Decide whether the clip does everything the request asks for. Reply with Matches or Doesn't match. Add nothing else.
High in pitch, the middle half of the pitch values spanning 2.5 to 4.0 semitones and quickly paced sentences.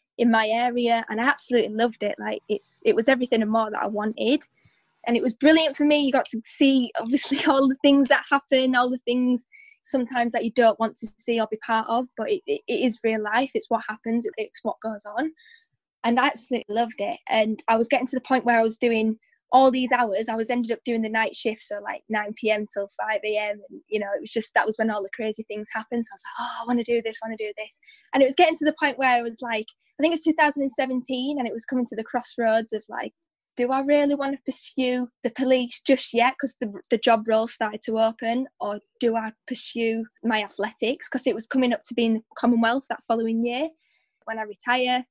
Matches